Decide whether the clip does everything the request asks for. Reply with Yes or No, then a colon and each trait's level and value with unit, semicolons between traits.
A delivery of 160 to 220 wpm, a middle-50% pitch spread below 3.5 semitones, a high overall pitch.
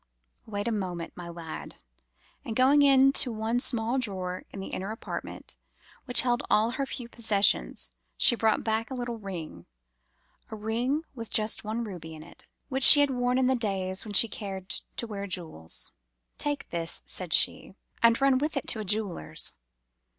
No: average, 170 wpm; average, 4.7 semitones; high, 220 Hz